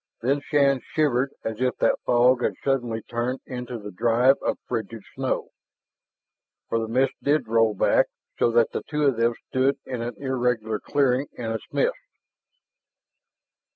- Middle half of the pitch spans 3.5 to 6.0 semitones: No, average, 2.8 semitones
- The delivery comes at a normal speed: Yes, average, 155 wpm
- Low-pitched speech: Yes, low, 125 Hz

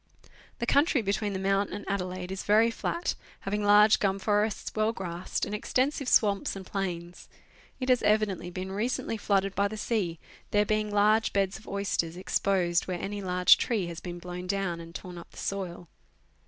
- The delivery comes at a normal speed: Yes, average, 180 wpm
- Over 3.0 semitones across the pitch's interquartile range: No, narrow, 2.6 semitones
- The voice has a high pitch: Yes, high, 200 Hz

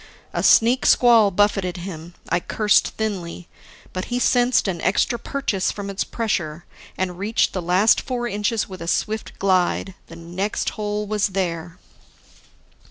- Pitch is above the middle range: Yes, high, 195 Hz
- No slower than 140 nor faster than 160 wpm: Yes, average, 150 wpm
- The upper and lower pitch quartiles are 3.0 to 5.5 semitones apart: Yes, average, 3.5 semitones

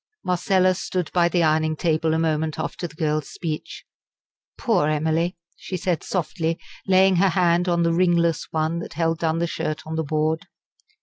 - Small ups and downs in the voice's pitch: Yes, narrow, 2.1 semitones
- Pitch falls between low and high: Yes, medium, 165 Hz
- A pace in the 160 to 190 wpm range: Yes, average, 175 wpm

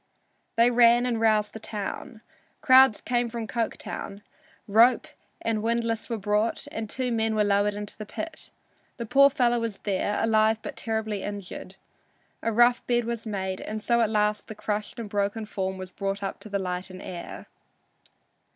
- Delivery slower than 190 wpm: Yes, average, 175 wpm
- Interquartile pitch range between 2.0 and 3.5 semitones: Yes, narrow, 2.4 semitones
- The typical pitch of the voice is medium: No, high, 220 Hz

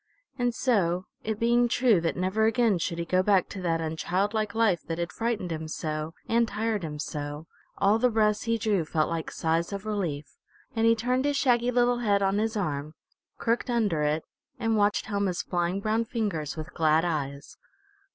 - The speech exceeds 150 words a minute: Yes, average, 190 wpm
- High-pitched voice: Yes, high, 200 Hz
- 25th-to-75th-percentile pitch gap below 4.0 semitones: No, wide, 5.5 semitones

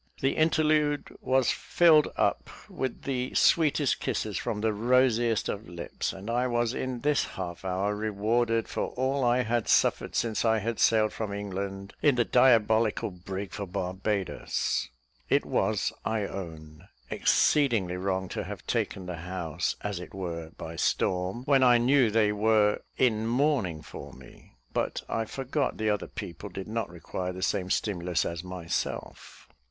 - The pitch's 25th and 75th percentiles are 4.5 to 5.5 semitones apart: Yes, average, 4.8 semitones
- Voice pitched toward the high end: No, low, 110 Hz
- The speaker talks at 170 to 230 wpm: No, average, 160 wpm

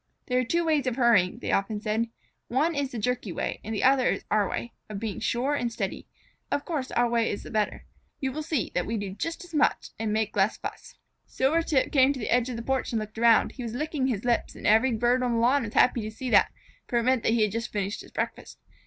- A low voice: No, high, 240 Hz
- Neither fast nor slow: No, fast, 260 wpm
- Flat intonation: No, average, 3.3 semitones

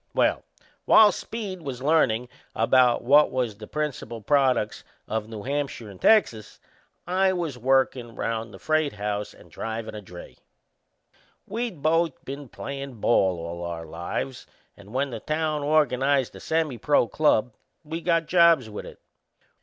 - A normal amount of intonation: No, wide, 5.9 semitones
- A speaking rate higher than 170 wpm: No, average, 145 wpm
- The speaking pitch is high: No, low, 135 Hz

